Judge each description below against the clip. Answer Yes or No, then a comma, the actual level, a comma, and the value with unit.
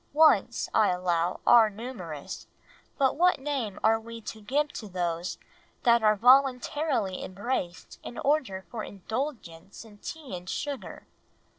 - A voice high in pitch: Yes, high, 225 Hz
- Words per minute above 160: No, slow, 135 wpm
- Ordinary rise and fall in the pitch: No, wide, 6.1 semitones